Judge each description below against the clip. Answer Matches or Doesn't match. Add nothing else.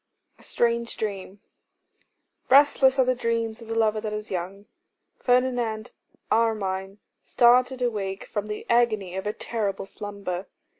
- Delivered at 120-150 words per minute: Matches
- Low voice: Doesn't match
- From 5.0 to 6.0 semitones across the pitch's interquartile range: Doesn't match